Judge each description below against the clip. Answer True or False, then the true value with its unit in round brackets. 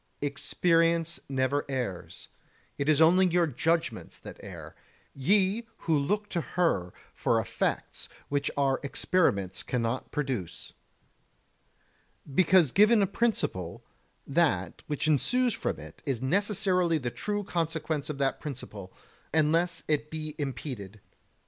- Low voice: False (155 Hz)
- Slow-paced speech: True (120 wpm)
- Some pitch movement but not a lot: True (4.8 semitones)